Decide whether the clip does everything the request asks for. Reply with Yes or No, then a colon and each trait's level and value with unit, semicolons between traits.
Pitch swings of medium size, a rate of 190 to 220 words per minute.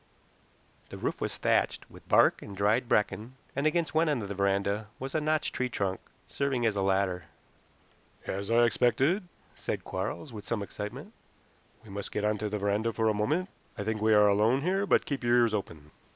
Yes: average, 4.7 semitones; average, 195 wpm